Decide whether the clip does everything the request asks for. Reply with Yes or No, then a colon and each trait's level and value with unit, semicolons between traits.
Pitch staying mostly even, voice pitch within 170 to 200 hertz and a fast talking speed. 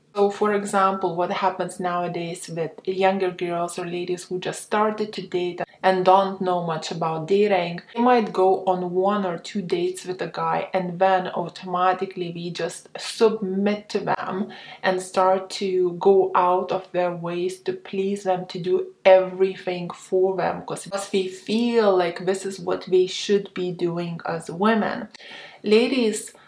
No: narrow, 1.6 semitones; medium, 185 Hz; average, 160 wpm